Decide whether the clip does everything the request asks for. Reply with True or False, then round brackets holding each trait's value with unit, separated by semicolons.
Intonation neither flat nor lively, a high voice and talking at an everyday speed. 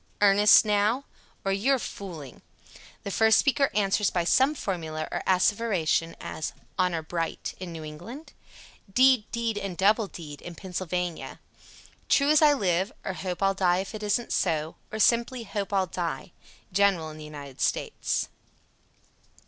True (4.4 semitones; 195 Hz; 150 wpm)